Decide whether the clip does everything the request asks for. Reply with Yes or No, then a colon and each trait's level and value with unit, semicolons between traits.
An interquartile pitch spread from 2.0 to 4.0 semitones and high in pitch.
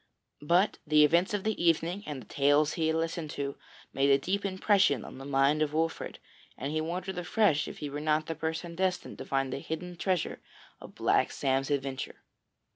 No: average, 3.7 semitones; medium, 160 Hz